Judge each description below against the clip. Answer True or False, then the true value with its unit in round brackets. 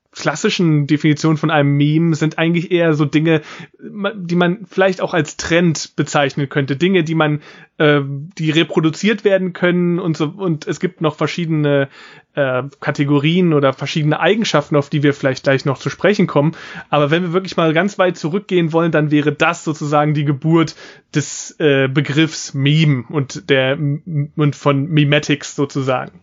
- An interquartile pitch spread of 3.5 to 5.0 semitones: False (2.7 semitones)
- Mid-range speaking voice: True (155 Hz)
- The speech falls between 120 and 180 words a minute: True (165 wpm)